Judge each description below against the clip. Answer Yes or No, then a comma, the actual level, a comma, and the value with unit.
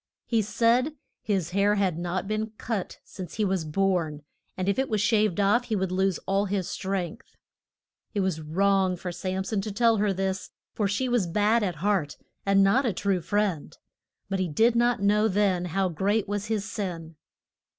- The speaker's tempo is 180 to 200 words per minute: Yes, average, 190 wpm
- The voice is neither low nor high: No, high, 195 Hz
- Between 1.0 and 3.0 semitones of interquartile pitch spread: Yes, narrow, 2.5 semitones